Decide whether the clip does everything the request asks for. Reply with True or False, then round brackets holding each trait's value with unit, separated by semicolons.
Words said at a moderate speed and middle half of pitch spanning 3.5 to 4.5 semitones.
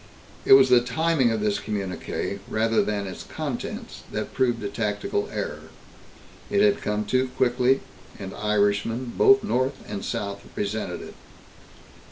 True (145 wpm; 4.1 semitones)